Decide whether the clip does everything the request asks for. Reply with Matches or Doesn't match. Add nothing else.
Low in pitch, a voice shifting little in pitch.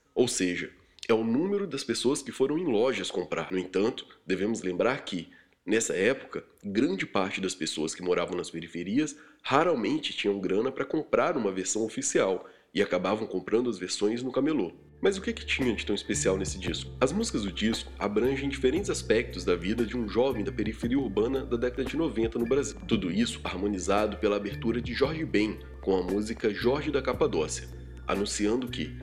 Doesn't match